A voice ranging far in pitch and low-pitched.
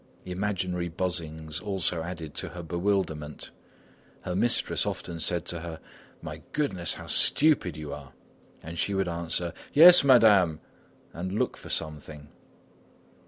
No: average, 3.3 semitones; very low, 85 Hz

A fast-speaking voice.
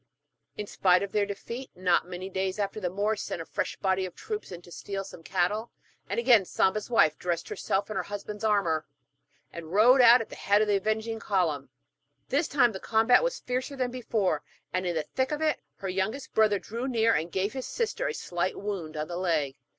Yes: fast, 210 wpm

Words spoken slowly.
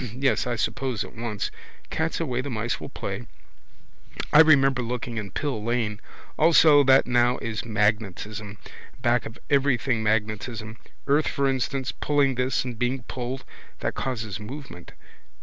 No: average, 145 wpm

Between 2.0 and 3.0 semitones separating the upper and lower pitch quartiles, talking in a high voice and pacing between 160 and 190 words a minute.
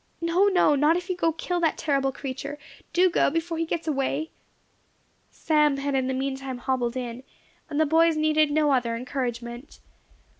No: average, 3.7 semitones; very high, 290 Hz; average, 180 wpm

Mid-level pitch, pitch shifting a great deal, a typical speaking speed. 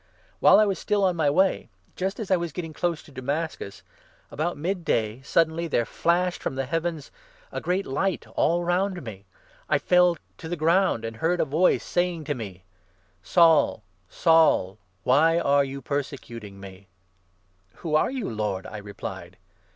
Yes: medium, 155 Hz; wide, 7.5 semitones; average, 185 wpm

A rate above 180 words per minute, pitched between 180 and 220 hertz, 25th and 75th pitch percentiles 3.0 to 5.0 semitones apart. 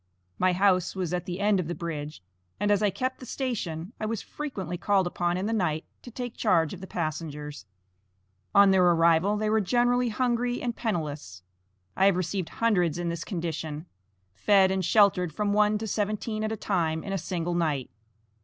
Yes: average, 190 wpm; high, 190 Hz; average, 4.2 semitones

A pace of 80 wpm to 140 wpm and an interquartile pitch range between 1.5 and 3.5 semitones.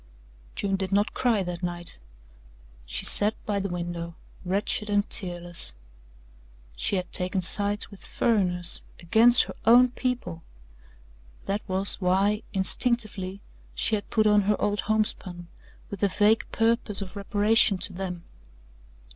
Yes: slow, 135 wpm; average, 2.7 semitones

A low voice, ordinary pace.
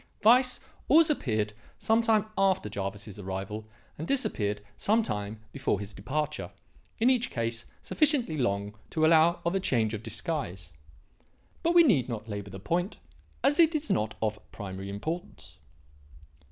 Yes: low, 120 Hz; average, 150 wpm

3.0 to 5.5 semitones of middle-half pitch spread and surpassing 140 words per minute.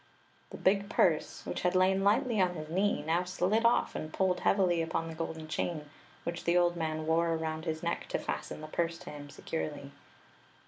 No: narrow, 2.6 semitones; average, 195 wpm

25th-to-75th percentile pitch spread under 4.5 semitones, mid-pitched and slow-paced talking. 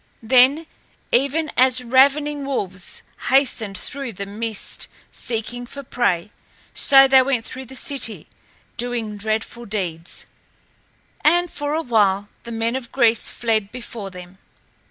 No: average, 4.1 semitones; high, 240 Hz; slow, 130 wpm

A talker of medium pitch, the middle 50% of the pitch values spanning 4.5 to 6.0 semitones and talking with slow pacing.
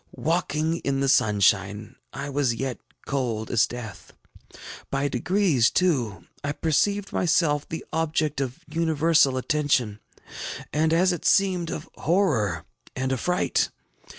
Yes: medium, 145 Hz; average, 5.1 semitones; slow, 125 wpm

